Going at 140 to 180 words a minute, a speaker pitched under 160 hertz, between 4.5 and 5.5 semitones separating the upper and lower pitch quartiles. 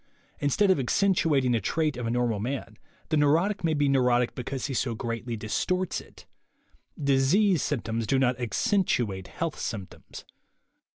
Yes: average, 160 wpm; low, 135 Hz; average, 5.0 semitones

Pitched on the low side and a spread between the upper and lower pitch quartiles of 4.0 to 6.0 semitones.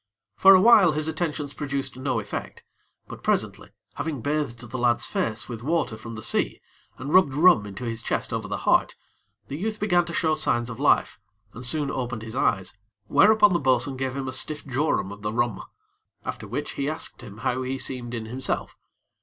Yes: low, 130 Hz; average, 4.7 semitones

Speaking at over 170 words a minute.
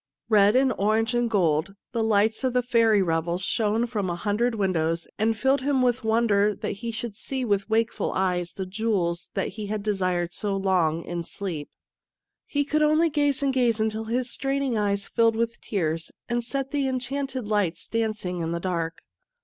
Yes: average, 190 wpm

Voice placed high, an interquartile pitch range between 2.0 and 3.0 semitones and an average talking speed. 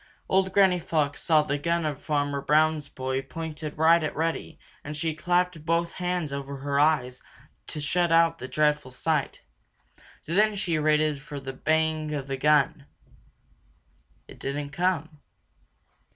No: medium, 155 Hz; narrow, 2.6 semitones; average, 150 wpm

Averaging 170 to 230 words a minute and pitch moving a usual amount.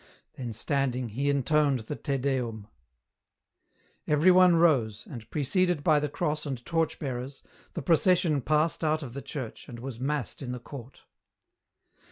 No: average, 160 wpm; average, 3.6 semitones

